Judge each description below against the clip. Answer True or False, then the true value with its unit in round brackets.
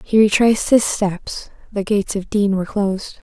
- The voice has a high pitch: True (205 Hz)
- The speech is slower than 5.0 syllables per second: False (5.2 syllables/s)